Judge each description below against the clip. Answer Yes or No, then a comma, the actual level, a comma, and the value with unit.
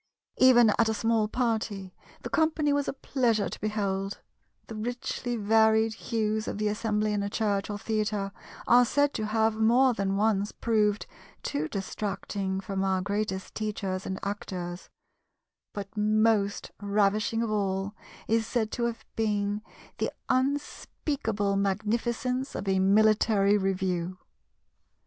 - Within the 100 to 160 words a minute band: Yes, slow, 135 wpm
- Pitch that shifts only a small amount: Yes, narrow, 2.2 semitones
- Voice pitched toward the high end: Yes, high, 215 Hz